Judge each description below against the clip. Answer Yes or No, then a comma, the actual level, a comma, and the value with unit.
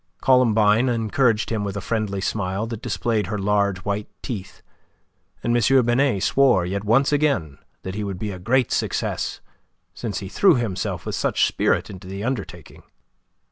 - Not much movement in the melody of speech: No, average, 3.5 semitones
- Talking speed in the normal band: Yes, average, 165 wpm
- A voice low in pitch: Yes, low, 105 Hz